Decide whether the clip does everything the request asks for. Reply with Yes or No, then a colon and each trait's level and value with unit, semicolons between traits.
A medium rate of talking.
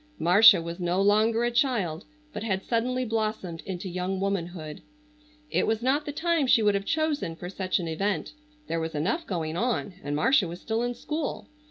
Yes: average, 190 wpm